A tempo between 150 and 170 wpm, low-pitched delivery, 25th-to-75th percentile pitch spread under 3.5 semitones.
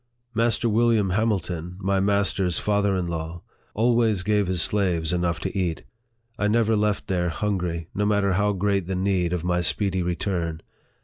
Yes: average, 165 wpm; very low, 95 Hz; average, 2.9 semitones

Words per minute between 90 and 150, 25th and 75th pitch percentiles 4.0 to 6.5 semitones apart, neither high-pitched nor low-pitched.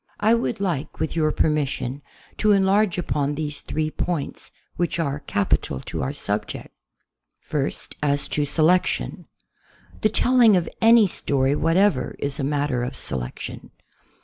Yes: average, 145 wpm; average, 5.2 semitones; medium, 155 Hz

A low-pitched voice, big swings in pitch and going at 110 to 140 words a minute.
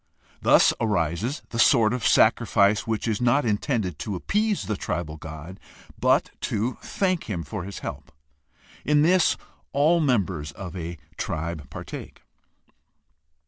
Yes: low, 105 Hz; wide, 6.8 semitones; slow, 135 wpm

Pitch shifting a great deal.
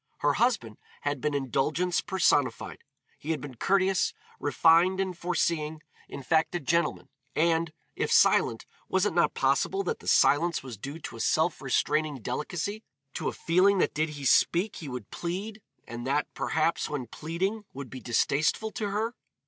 No: average, 4.7 semitones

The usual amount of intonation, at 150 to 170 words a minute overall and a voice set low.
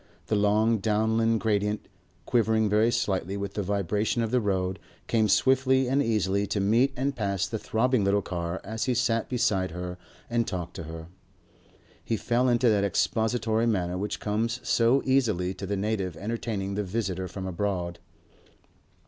Yes: average, 3.1 semitones; average, 165 wpm; low, 105 Hz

